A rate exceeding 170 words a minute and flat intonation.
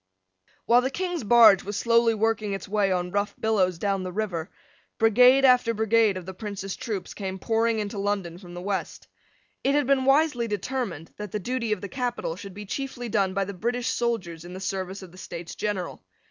No: average, 200 wpm; average, 3.9 semitones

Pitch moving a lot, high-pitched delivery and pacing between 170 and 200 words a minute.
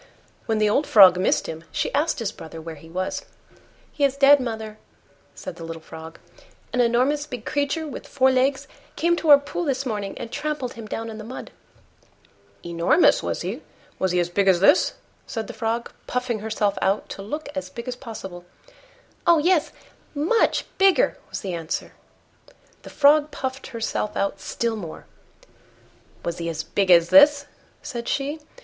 Yes: wide, 6.7 semitones; high, 235 Hz; average, 175 wpm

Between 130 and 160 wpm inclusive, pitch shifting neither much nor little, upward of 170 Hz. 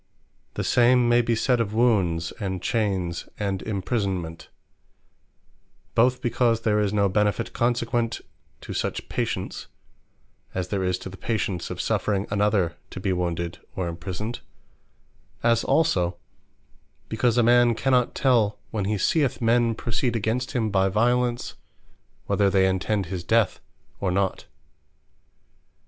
No: slow, 135 wpm; average, 3.9 semitones; low, 105 Hz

